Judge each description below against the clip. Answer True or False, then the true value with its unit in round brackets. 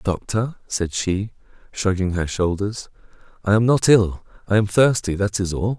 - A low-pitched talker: True (100 Hz)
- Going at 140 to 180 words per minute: True (165 wpm)